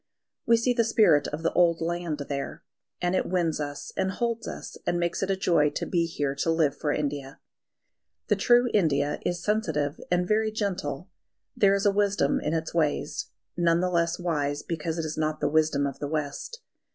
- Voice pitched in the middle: Yes, medium, 170 Hz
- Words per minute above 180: Yes, average, 200 wpm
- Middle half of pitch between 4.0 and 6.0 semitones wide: Yes, average, 4.5 semitones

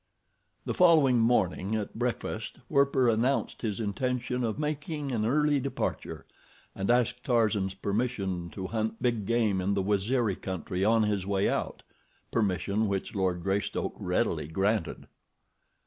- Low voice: Yes, low, 110 Hz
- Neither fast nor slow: No, slow, 130 wpm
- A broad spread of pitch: No, average, 4.2 semitones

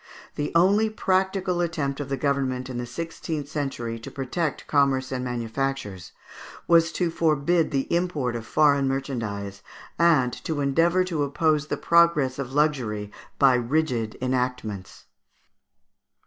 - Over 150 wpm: No, slow, 135 wpm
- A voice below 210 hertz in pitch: Yes, medium, 140 Hz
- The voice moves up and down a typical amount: Yes, average, 4.7 semitones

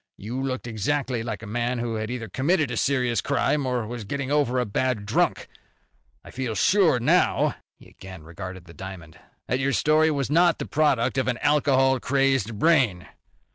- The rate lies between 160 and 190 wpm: Yes, average, 180 wpm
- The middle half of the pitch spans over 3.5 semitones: Yes, average, 4.1 semitones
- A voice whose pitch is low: Yes, low, 125 Hz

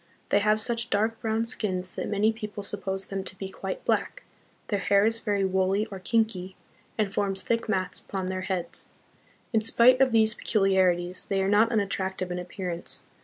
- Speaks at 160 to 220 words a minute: Yes, average, 180 wpm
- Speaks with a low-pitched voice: No, high, 200 Hz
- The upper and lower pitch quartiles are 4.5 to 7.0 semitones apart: No, average, 2.7 semitones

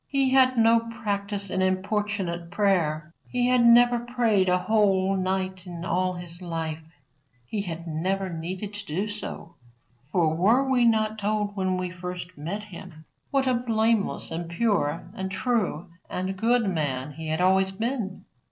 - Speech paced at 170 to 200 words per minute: No, average, 155 wpm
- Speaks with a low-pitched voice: No, high, 190 Hz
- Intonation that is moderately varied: Yes, average, 3.9 semitones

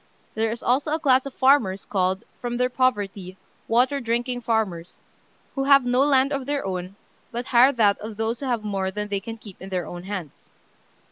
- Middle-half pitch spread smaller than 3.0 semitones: No, average, 4.7 semitones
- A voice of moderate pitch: No, high, 230 Hz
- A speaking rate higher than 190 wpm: Yes, average, 200 wpm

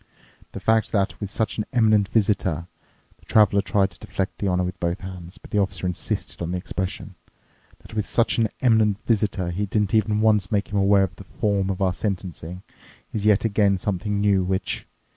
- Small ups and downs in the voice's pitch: Yes, narrow, 2.3 semitones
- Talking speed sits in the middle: Yes, average, 190 wpm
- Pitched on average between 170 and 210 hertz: No, low, 100 Hz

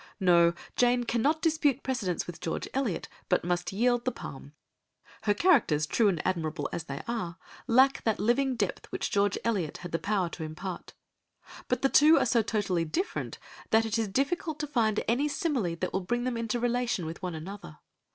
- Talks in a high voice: Yes, high, 220 Hz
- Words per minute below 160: No, average, 190 wpm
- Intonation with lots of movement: Yes, wide, 6.0 semitones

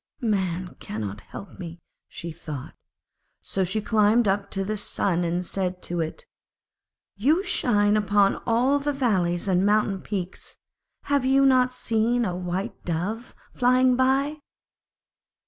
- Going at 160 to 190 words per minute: No, slow, 135 wpm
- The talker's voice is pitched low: No, high, 205 Hz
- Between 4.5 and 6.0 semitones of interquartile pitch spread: Yes, wide, 5.5 semitones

